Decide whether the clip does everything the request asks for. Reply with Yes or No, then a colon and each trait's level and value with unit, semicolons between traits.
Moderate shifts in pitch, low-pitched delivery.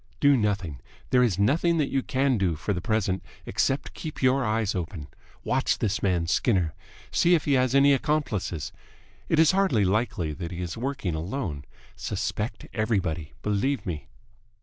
No: wide, 7.1 semitones; low, 105 Hz